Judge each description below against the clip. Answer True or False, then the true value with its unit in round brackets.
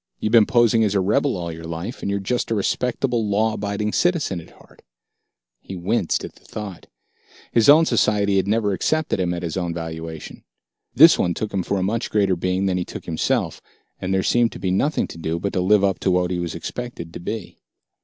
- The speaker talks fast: True (225 wpm)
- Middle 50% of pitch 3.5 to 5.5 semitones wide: True (4.1 semitones)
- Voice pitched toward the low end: True (100 Hz)